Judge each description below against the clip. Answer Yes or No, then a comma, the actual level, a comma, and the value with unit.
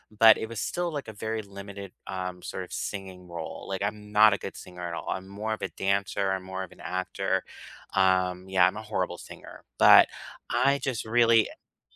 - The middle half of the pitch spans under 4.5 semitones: Yes, average, 2.8 semitones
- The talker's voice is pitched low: Yes, low, 100 Hz